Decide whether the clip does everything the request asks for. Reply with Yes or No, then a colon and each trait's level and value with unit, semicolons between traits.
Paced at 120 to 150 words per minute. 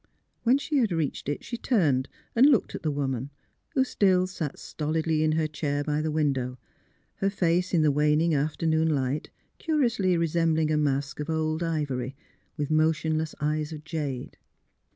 No: average, 165 wpm